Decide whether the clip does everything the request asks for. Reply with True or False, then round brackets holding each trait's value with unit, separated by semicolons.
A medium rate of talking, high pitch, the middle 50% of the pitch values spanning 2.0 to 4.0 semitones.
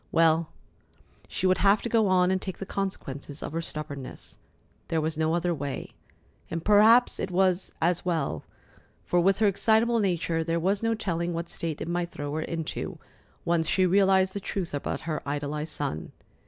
False (180 wpm; 170 Hz; 3.4 semitones)